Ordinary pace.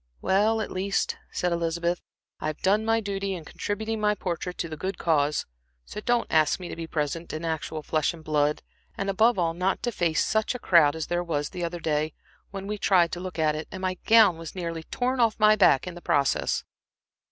No: fast, 220 wpm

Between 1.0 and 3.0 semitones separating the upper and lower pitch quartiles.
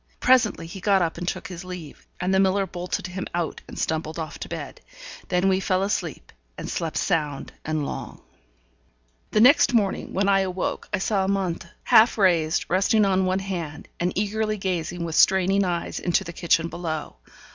Yes: narrow, 2.6 semitones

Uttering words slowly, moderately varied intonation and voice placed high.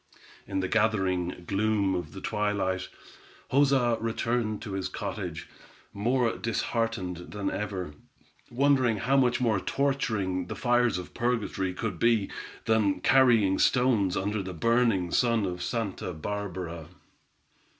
No: slow, 125 wpm; average, 4.1 semitones; low, 105 Hz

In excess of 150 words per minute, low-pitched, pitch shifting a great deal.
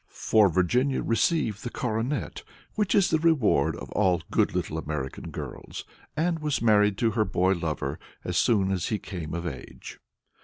Yes: average, 165 wpm; low, 105 Hz; wide, 6.6 semitones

